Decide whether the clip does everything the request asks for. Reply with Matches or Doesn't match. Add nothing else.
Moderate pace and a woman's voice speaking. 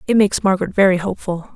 Matches